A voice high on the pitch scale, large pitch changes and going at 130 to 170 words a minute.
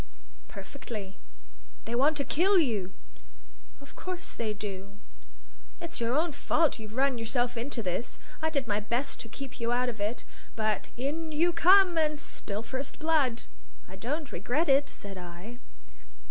Yes: very high, 250 Hz; wide, 5.9 semitones; average, 160 wpm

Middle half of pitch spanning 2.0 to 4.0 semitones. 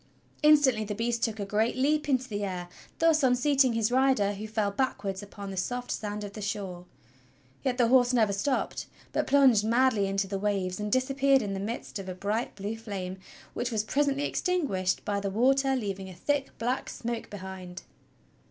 No: average, 4.5 semitones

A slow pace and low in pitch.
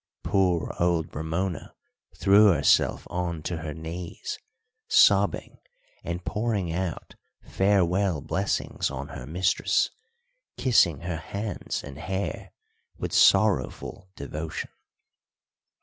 Yes: slow, 100 wpm; very low, 90 Hz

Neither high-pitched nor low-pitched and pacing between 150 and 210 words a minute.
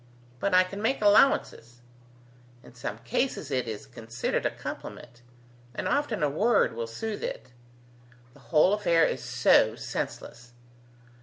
No: medium, 150 Hz; average, 140 wpm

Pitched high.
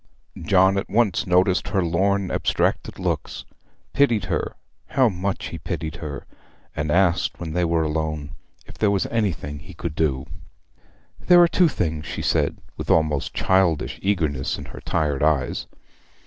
No: very low, 85 Hz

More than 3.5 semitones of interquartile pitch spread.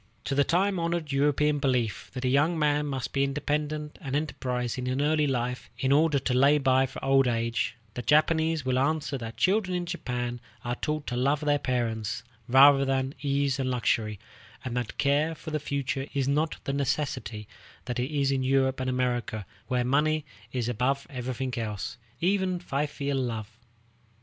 No: average, 3.0 semitones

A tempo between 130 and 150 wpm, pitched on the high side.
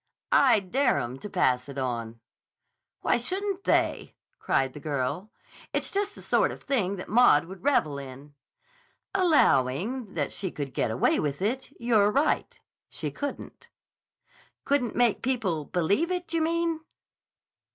Yes: average, 145 wpm; high, 200 Hz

